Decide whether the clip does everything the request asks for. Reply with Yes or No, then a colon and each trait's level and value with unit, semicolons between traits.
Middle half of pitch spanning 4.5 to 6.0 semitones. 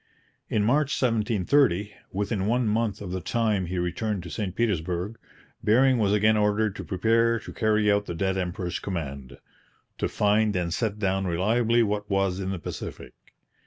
No: average, 3.2 semitones